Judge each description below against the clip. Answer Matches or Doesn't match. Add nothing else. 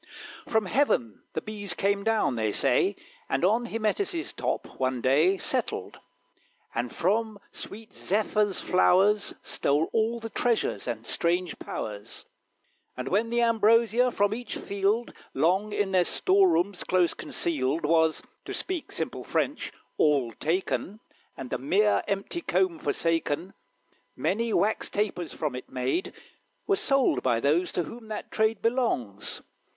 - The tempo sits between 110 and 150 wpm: Matches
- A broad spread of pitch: Matches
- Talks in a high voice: Matches